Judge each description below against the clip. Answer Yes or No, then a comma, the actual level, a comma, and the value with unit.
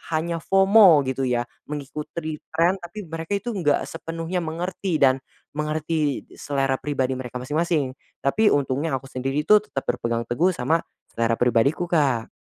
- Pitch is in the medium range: Yes, medium, 150 Hz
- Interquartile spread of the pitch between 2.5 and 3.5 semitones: No, average, 4.2 semitones